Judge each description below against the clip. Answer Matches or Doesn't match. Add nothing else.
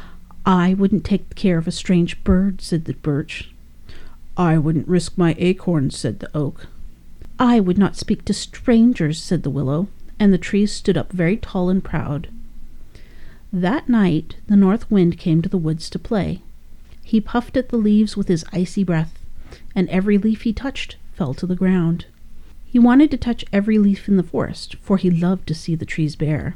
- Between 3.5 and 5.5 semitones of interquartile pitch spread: Matches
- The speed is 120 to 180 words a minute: Doesn't match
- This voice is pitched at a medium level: Matches